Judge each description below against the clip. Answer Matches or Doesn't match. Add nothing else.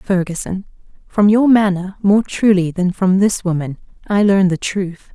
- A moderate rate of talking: Matches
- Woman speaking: Matches